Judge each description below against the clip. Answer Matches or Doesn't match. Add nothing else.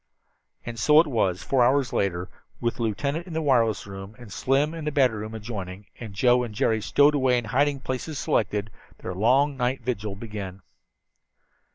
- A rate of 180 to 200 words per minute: Matches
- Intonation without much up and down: Doesn't match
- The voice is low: Matches